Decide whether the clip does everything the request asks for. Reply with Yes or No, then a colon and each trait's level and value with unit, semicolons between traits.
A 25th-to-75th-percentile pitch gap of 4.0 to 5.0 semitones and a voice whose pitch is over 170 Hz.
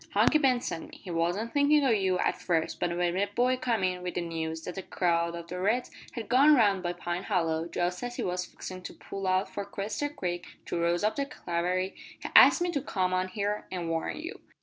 Yes: average, 4.6 semitones; medium, 185 Hz